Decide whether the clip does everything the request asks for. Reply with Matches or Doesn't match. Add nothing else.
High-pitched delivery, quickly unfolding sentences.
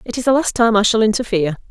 Matches